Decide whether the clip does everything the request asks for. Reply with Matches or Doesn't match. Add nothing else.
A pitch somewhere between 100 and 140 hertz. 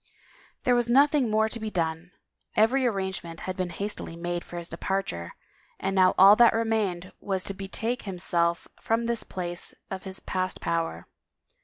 Doesn't match